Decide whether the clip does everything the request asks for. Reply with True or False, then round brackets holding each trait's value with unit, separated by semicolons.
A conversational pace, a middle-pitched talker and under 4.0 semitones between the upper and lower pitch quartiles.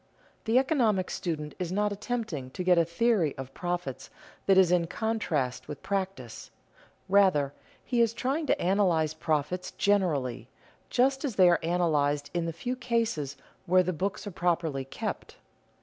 False (155 wpm; 180 Hz; 5.4 semitones)